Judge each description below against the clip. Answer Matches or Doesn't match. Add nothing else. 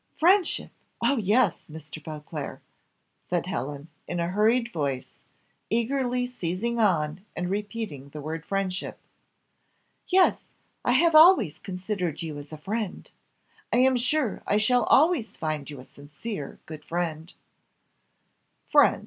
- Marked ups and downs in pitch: Matches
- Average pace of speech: Doesn't match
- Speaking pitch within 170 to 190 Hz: Matches